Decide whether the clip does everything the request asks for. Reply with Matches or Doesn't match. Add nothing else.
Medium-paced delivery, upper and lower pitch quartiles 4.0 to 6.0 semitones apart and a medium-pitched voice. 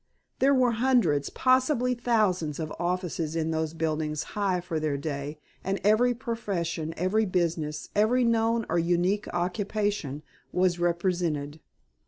Doesn't match